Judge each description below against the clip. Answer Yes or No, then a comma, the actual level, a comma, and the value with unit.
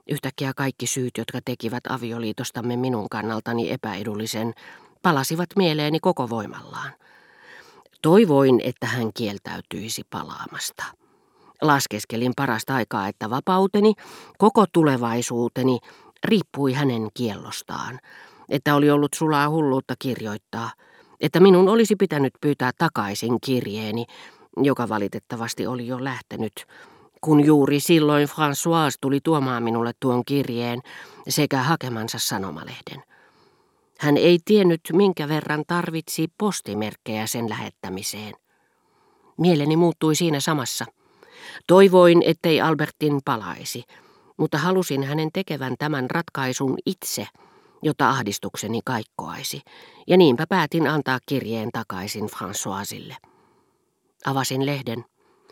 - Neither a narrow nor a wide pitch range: No, wide, 6.0 semitones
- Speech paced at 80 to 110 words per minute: Yes, average, 100 wpm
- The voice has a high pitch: No, medium, 140 Hz